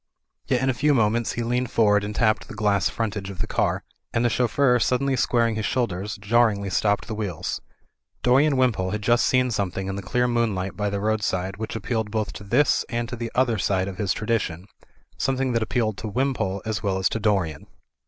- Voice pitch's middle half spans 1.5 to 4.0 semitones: Yes, average, 3.2 semitones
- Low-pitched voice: Yes, low, 110 Hz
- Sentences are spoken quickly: Yes, fast, 210 wpm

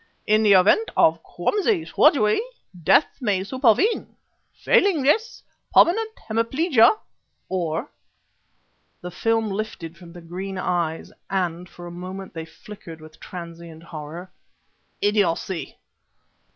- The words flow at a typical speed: No, slow, 110 wpm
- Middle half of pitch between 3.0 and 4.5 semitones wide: No, average, 5.2 semitones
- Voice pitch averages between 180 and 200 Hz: Yes, high, 190 Hz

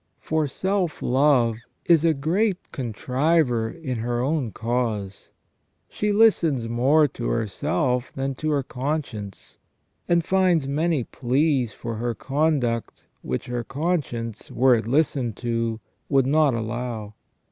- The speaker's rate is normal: No, slow, 130 wpm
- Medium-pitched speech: No, low, 130 Hz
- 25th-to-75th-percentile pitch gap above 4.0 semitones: Yes, average, 5.0 semitones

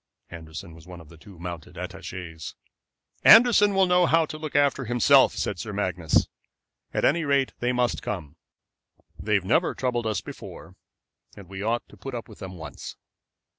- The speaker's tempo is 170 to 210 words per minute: Yes, average, 175 wpm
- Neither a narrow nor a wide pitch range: No, wide, 8.2 semitones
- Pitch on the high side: No, low, 110 Hz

